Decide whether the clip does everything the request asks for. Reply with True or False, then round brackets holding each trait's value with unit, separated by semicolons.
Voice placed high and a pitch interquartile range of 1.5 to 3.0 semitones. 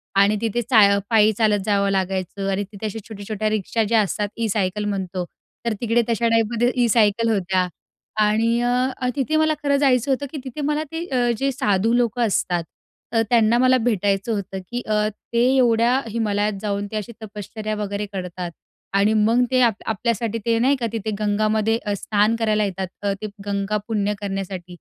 True (215 Hz; 2.7 semitones)